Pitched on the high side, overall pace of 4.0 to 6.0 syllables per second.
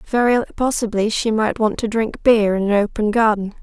Yes: high, 220 Hz; 5.1 syllables/s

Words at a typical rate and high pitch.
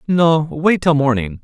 No: average, 170 wpm; medium, 150 Hz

